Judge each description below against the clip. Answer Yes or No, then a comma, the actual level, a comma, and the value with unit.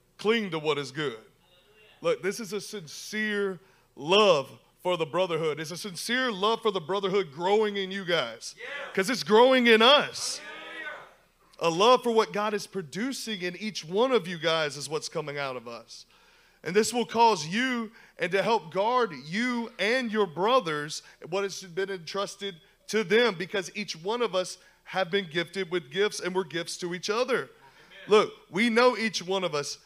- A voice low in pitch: No, high, 200 Hz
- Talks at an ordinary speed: Yes, average, 185 wpm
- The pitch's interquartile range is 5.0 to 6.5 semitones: No, average, 4.2 semitones